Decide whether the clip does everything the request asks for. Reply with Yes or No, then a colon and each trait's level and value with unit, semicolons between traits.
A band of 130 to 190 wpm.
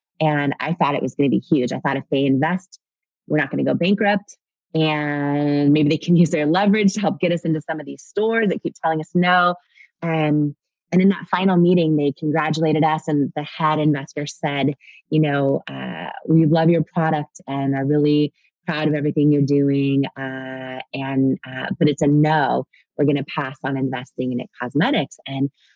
No: fast, 205 wpm